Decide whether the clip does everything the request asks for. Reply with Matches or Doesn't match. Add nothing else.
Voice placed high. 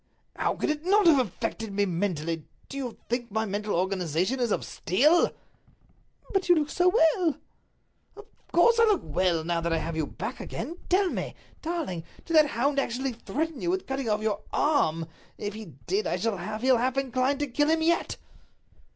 Matches